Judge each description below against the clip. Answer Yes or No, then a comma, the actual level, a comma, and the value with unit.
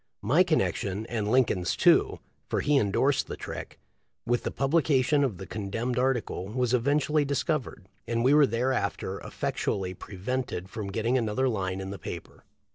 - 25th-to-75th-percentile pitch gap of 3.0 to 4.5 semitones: No, average, 5.1 semitones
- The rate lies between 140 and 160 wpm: No, average, 180 wpm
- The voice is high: No, low, 120 Hz